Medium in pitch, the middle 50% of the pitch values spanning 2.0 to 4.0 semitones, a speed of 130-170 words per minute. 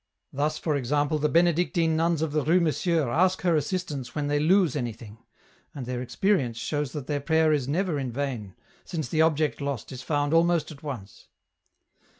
No: medium, 150 Hz; average, 3.2 semitones; average, 180 wpm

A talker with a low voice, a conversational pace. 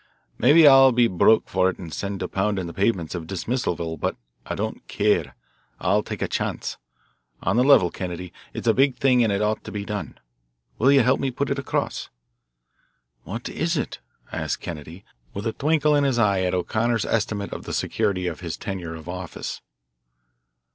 Yes: low, 105 Hz; average, 190 wpm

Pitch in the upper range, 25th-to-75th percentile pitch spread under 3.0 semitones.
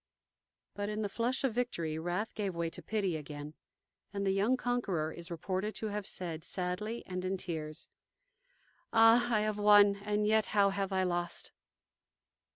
No: high, 200 Hz; average, 3.5 semitones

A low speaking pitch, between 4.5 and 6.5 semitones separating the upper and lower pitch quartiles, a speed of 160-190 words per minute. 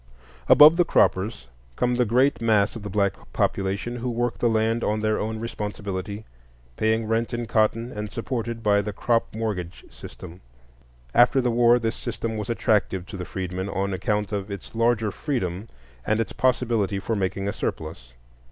No: low, 110 Hz; average, 2.8 semitones; average, 170 wpm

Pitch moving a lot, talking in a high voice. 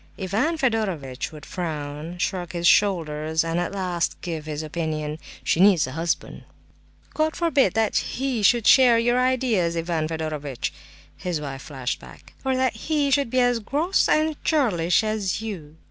No: wide, 7.6 semitones; medium, 180 Hz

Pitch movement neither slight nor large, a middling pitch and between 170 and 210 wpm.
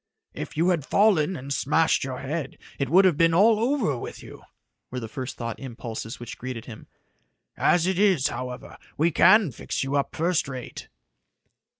No: wide, 6.0 semitones; medium, 150 Hz; average, 185 wpm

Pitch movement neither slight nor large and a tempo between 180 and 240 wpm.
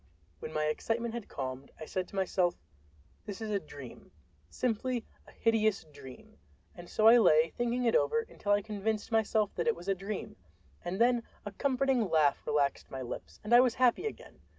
No: wide, 6.5 semitones; average, 185 wpm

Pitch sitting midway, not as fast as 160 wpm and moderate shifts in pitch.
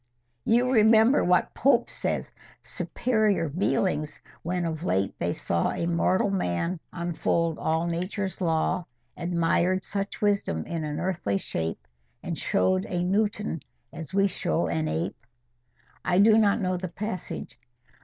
Yes: medium, 175 Hz; slow, 135 wpm; average, 4.4 semitones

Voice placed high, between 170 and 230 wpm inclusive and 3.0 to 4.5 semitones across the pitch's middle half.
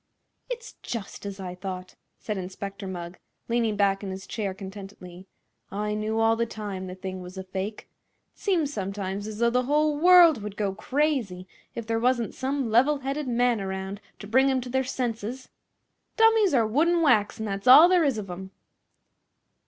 No: high, 215 Hz; average, 185 wpm; average, 5.3 semitones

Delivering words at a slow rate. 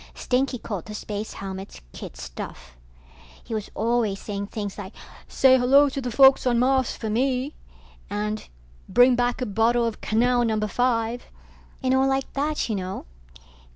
No: average, 160 wpm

